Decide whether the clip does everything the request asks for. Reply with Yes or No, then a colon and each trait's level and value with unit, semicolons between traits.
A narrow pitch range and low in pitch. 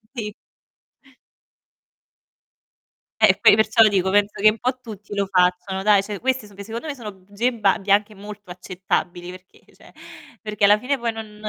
No: narrow, 2.3 semitones; high, 205 Hz